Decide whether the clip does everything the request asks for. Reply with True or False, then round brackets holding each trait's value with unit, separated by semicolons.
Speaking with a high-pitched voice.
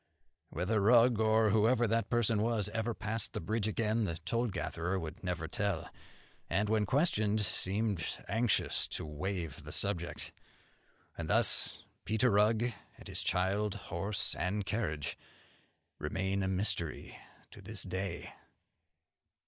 False (105 Hz)